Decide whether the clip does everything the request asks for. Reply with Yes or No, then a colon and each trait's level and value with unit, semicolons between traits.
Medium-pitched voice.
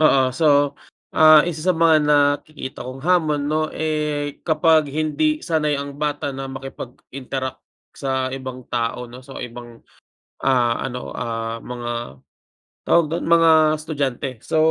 Yes: medium, 145 Hz